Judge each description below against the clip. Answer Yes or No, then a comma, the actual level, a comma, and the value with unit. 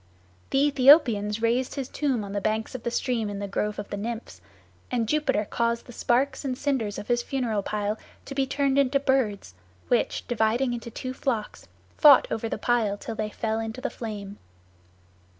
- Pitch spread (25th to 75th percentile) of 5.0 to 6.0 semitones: No, average, 3.7 semitones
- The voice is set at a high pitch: Yes, high, 235 Hz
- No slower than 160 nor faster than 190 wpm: Yes, average, 185 wpm